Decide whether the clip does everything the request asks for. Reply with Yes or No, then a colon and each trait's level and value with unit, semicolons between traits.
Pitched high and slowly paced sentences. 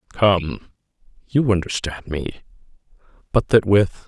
No: very low, 95 Hz; slow, 90 wpm